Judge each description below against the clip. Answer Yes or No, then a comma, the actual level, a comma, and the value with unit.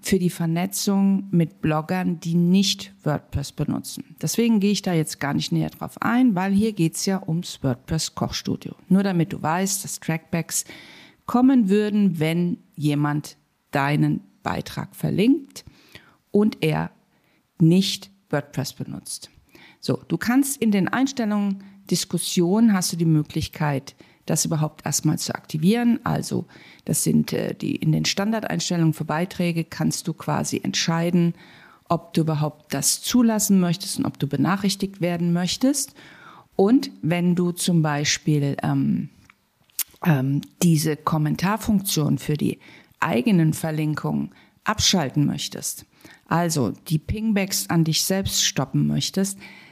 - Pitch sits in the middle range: Yes, medium, 175 Hz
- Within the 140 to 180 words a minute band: No, average, 130 wpm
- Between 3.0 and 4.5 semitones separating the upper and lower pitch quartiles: Yes, average, 4.2 semitones